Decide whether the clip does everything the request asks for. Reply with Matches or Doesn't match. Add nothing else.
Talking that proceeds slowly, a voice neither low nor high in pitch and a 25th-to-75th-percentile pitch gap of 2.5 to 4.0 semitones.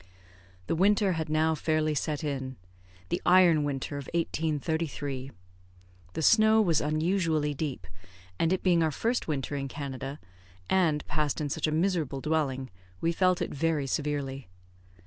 Doesn't match